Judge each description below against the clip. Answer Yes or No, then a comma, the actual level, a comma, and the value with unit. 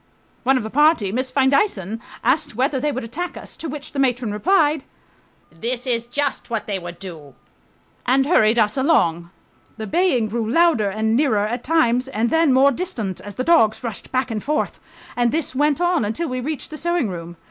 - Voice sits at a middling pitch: No, very high, 255 Hz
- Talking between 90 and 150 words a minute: No, average, 195 wpm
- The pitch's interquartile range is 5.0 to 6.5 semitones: Yes, wide, 5.4 semitones